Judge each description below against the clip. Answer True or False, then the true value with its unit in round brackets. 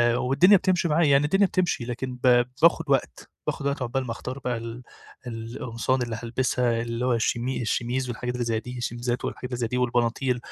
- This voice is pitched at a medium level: False (125 Hz)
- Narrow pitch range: True (2.0 semitones)